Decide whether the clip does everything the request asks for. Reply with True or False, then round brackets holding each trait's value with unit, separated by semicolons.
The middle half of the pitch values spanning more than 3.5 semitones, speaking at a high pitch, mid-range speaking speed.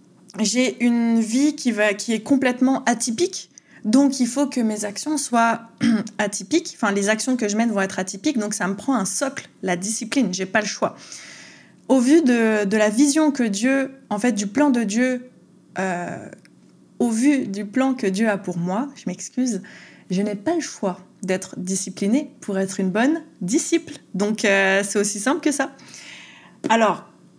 True (4.7 semitones; 230 Hz; 185 wpm)